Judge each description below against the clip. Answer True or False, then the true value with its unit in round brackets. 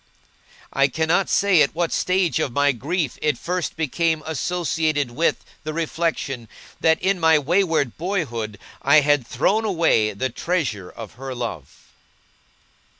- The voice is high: False (155 Hz)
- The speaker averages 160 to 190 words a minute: False (140 wpm)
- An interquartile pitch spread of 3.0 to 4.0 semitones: False (4.6 semitones)